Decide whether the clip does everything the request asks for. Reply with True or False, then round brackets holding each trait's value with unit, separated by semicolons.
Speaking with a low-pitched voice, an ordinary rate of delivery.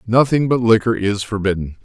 True (110 Hz; 165 wpm)